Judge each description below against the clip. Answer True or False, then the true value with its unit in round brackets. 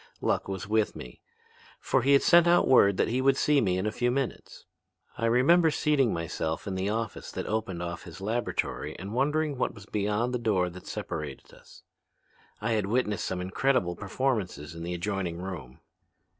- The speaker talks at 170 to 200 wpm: True (185 wpm)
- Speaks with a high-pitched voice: False (105 Hz)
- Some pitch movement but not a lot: False (5.7 semitones)